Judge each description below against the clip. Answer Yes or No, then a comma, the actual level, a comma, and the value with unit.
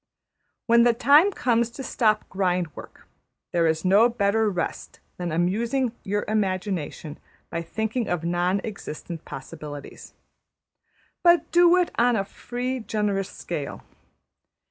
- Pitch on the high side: Yes, high, 205 Hz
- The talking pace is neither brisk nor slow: No, slow, 125 wpm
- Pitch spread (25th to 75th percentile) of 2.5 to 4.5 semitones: No, average, 5.1 semitones